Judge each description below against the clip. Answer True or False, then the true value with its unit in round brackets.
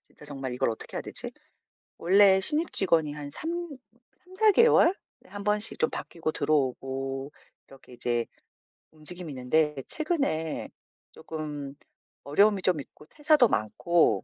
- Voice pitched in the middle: True (160 Hz)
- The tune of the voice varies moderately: False (6.8 semitones)